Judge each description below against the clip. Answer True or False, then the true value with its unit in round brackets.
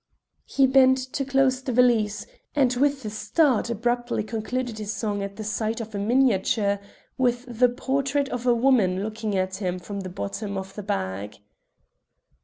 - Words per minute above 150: True (170 wpm)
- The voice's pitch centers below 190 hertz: False (225 Hz)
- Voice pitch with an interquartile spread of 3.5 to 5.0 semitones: True (4.1 semitones)